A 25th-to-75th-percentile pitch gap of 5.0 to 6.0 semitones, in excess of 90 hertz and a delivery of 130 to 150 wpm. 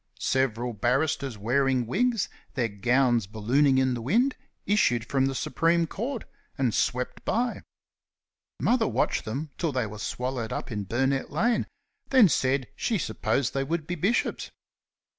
Yes: wide, 5.6 semitones; low, 135 Hz; average, 145 wpm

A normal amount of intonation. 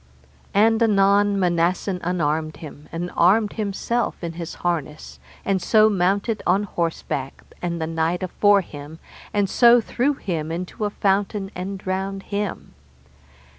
Yes: average, 3.3 semitones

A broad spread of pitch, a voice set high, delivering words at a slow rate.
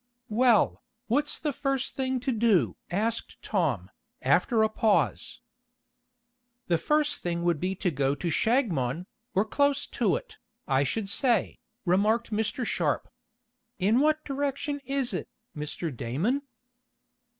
Yes: wide, 7.9 semitones; high, 220 Hz; slow, 130 wpm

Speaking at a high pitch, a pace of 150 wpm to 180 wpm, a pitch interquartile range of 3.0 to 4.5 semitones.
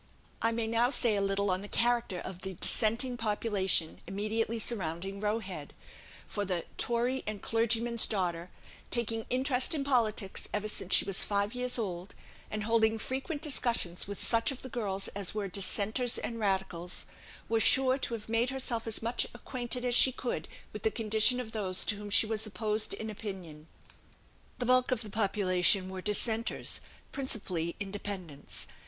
Yes: high, 215 Hz; average, 170 wpm; average, 3.4 semitones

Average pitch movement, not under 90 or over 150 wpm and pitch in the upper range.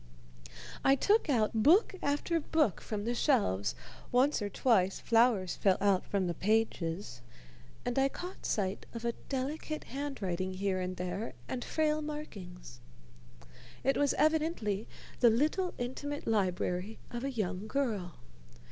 No: wide, 7.1 semitones; average, 140 wpm; high, 225 Hz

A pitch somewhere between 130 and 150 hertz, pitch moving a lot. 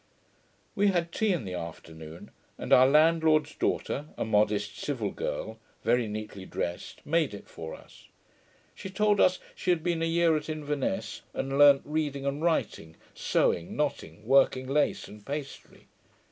Yes: medium, 140 Hz; wide, 7.3 semitones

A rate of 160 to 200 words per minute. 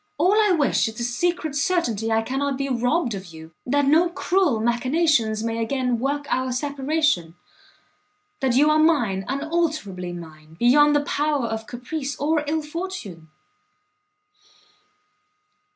No: slow, 135 wpm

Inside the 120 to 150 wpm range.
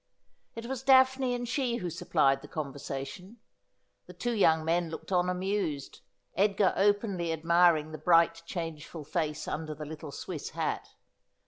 Yes: average, 145 wpm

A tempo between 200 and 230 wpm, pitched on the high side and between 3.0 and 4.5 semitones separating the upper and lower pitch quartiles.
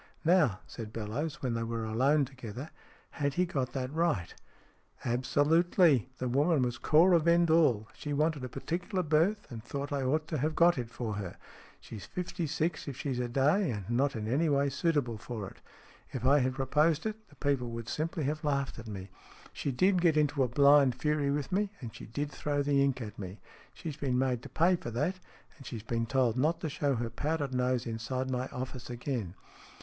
No: fast, 205 wpm; medium, 140 Hz; average, 4.2 semitones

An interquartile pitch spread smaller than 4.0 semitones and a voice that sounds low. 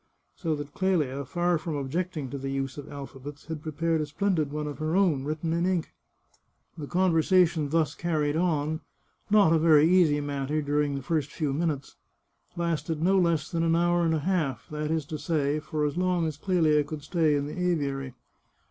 No: average, 2.7 semitones; medium, 155 Hz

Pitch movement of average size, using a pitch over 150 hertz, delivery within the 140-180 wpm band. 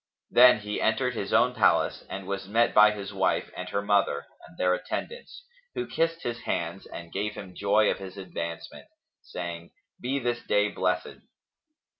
No: average, 4.0 semitones; low, 105 Hz; average, 170 wpm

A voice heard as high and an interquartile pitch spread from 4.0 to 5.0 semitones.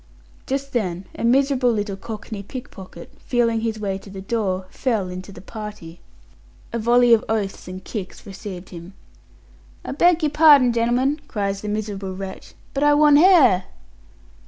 Yes: high, 220 Hz; average, 4.7 semitones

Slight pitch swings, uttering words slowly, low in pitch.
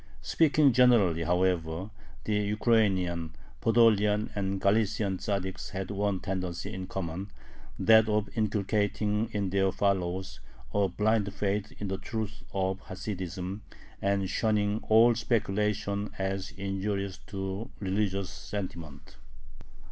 Yes: narrow, 2.0 semitones; slow, 110 wpm; low, 100 Hz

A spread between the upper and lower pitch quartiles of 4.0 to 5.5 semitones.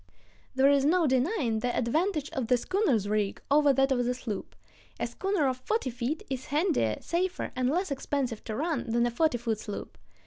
Yes: average, 4.6 semitones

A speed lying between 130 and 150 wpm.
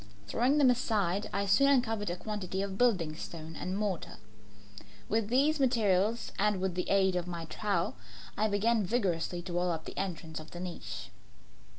No: average, 175 wpm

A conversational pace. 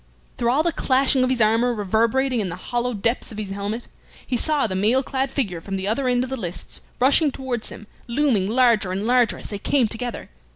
No: fast, 220 wpm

